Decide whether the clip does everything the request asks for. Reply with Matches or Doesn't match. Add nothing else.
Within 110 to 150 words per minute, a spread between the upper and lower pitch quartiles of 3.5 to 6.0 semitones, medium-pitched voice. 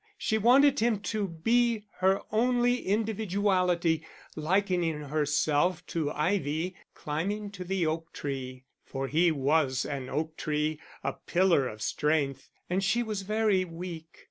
Matches